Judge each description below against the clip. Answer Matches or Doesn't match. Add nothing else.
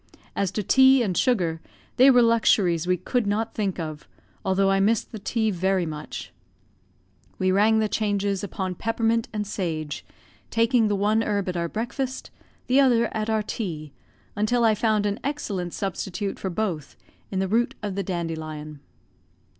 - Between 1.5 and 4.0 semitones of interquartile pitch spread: Matches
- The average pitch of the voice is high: Matches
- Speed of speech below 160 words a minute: Doesn't match